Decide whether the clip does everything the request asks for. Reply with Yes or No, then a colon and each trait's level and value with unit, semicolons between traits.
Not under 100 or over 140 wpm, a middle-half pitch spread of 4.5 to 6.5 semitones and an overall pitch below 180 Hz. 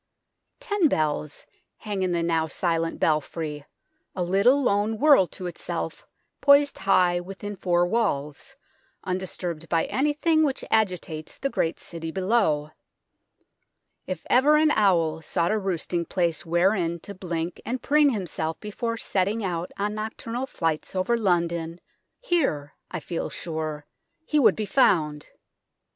No: slow, 135 wpm; average, 5.1 semitones; medium, 185 Hz